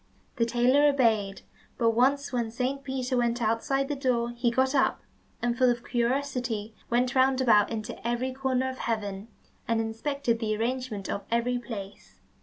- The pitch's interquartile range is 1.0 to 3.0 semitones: Yes, narrow, 2.4 semitones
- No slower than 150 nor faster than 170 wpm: Yes, average, 165 wpm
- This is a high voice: Yes, high, 240 Hz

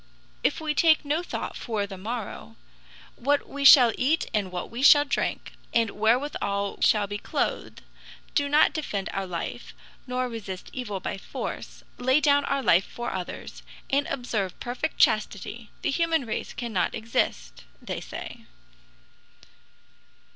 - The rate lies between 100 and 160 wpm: Yes, average, 145 wpm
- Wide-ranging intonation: Yes, wide, 5.9 semitones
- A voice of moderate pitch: No, high, 240 Hz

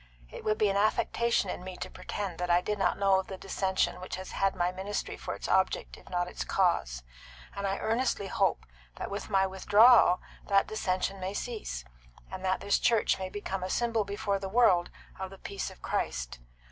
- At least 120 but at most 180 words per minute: No, average, 200 wpm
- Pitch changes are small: Yes, narrow, 2.0 semitones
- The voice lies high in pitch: Yes, high, 195 Hz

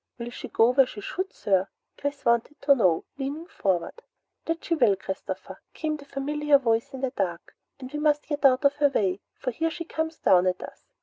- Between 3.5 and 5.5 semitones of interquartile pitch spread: Yes, average, 5.0 semitones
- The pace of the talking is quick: Yes, fast, 210 wpm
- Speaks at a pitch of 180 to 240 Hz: No, very high, 275 Hz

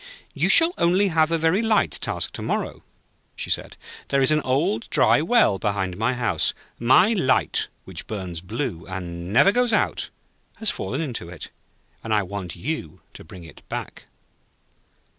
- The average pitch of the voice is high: No, low, 120 Hz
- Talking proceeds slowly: No, average, 165 wpm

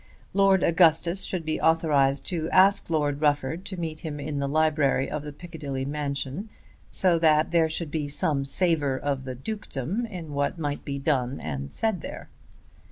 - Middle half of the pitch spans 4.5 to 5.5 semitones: No, average, 3.2 semitones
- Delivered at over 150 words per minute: Yes, average, 170 wpm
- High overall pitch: No, medium, 155 Hz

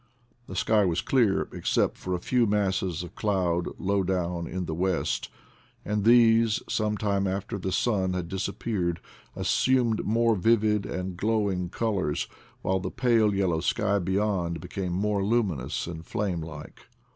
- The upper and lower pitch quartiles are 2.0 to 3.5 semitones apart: Yes, average, 3.1 semitones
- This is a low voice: Yes, very low, 95 Hz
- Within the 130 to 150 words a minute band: No, average, 160 wpm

